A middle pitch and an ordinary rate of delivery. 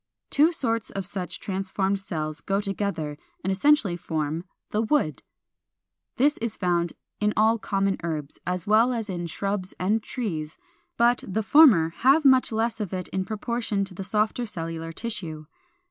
No: high, 200 Hz; average, 160 wpm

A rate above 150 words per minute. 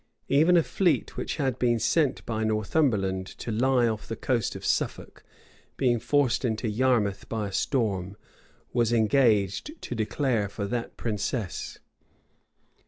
No: average, 140 wpm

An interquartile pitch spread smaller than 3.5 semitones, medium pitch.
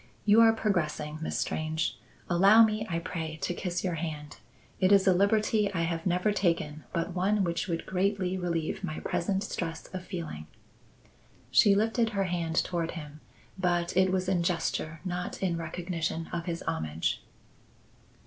Yes: average, 2.7 semitones; medium, 175 Hz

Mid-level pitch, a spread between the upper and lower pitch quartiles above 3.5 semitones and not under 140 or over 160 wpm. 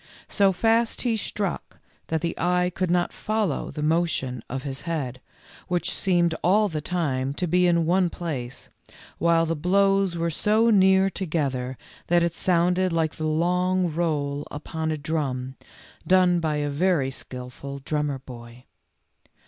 Yes: medium, 170 Hz; average, 3.9 semitones; average, 150 wpm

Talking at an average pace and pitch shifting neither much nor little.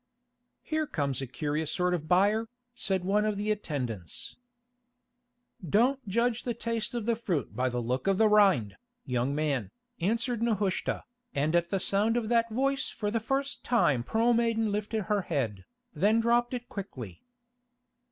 No: average, 160 wpm; wide, 7.3 semitones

